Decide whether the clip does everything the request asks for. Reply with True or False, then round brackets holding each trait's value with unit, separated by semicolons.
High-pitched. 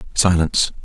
False (85 Hz)